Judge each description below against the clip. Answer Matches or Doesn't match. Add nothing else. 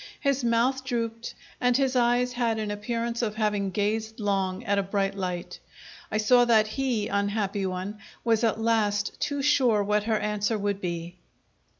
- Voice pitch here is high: Matches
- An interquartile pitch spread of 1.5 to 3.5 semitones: Matches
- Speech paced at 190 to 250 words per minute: Doesn't match